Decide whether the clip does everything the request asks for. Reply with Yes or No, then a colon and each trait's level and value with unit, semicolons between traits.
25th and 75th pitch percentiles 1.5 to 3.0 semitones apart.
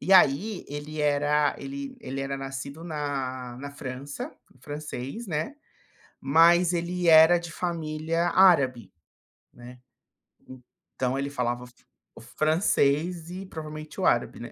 No: average, 3.9 semitones